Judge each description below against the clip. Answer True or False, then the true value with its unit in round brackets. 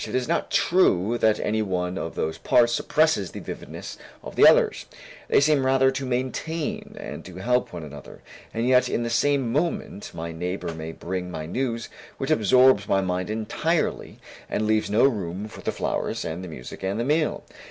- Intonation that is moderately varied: False (6.4 semitones)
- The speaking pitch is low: True (110 Hz)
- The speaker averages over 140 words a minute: True (190 wpm)